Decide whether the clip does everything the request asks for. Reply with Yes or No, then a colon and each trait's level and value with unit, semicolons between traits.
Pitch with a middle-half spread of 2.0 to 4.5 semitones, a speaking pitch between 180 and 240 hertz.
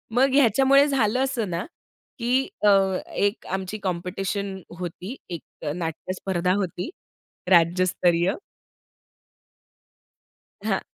No: average, 4.9 semitones; high, 190 Hz